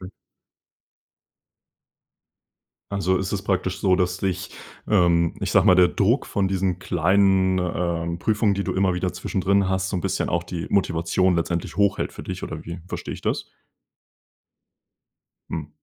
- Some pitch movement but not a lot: No, narrow, 1.7 semitones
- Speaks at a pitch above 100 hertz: No, very low, 95 Hz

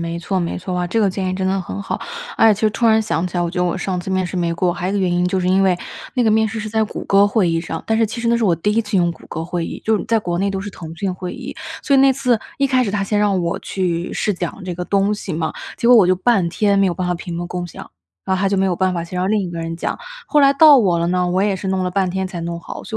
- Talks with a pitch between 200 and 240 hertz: No, high, 190 Hz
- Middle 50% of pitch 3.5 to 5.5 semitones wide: No, average, 3.0 semitones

